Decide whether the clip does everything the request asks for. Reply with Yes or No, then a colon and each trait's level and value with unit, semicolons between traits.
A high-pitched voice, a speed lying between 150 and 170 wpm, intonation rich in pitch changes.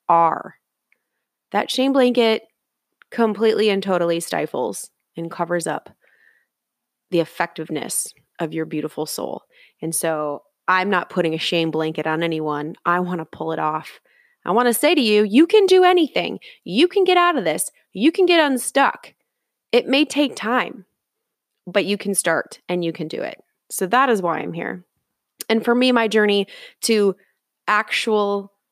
Yes: high, 200 Hz; average, 165 wpm; wide, 6.9 semitones